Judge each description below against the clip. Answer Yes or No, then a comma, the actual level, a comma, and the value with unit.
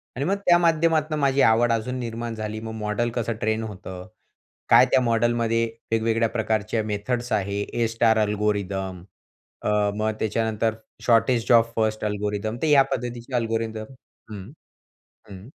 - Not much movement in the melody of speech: Yes, narrow, 2.0 semitones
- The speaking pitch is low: Yes, low, 115 Hz